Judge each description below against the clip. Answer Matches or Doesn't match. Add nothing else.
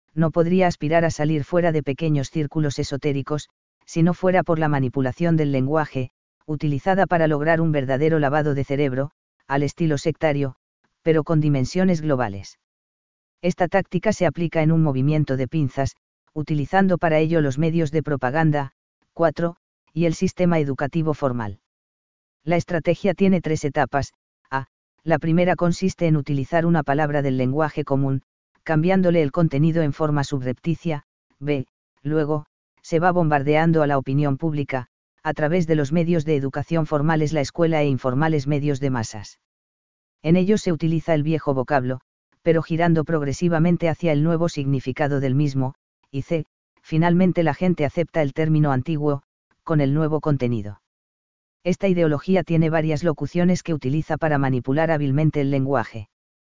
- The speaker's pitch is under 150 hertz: Doesn't match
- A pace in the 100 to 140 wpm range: Doesn't match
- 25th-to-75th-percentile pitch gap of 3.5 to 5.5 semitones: Doesn't match